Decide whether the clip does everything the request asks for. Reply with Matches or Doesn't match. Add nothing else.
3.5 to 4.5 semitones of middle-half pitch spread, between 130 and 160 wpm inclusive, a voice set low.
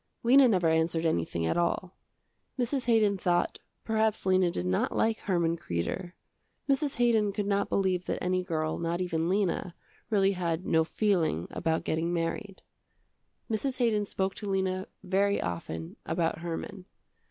Doesn't match